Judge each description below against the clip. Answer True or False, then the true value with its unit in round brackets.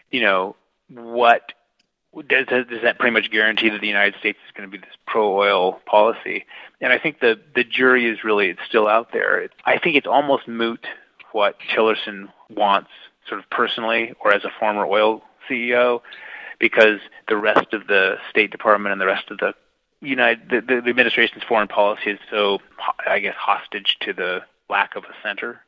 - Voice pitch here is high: False (120 Hz)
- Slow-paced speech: False (180 wpm)